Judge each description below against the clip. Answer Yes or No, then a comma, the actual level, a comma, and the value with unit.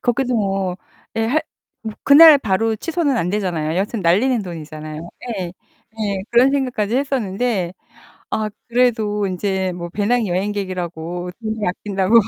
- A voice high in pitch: Yes, high, 205 Hz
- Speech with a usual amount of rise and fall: Yes, average, 4.7 semitones